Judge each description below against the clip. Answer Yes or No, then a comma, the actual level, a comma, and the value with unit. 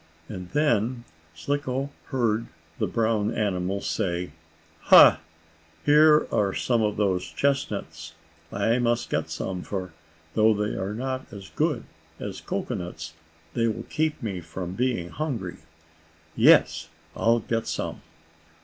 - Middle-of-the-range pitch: No, low, 110 Hz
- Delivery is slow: Yes, slow, 125 wpm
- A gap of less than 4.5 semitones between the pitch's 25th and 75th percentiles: No, wide, 5.4 semitones